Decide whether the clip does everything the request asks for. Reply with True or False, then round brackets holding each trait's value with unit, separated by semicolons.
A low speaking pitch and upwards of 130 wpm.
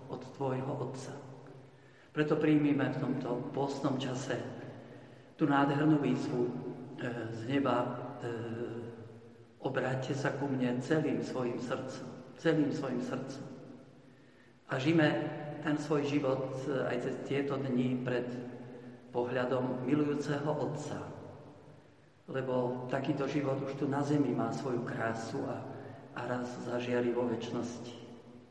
False (130 Hz; 115 wpm)